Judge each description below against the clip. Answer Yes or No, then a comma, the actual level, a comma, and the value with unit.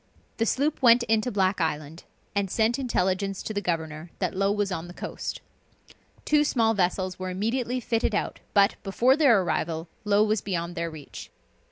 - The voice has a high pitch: Yes, high, 200 Hz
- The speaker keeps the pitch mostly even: No, average, 4.3 semitones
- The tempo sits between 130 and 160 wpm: No, average, 175 wpm